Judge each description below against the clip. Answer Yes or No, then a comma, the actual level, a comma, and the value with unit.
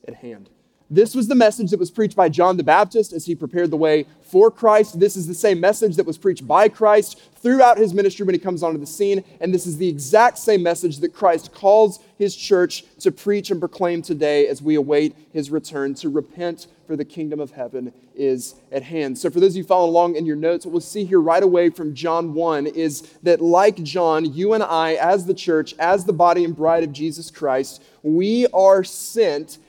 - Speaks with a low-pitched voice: No, medium, 175 Hz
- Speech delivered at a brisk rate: Yes, fast, 225 wpm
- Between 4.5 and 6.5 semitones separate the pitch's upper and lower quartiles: No, average, 4.1 semitones